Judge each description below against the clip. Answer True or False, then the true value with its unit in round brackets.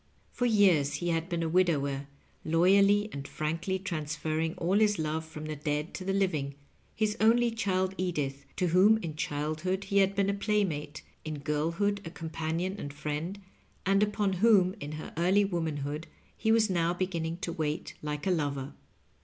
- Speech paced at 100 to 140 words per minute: False (170 wpm)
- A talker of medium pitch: True (170 Hz)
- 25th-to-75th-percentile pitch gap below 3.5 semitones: False (4.3 semitones)